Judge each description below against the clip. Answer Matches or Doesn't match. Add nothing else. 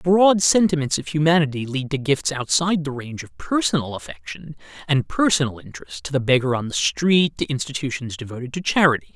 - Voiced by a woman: Doesn't match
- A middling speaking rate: Matches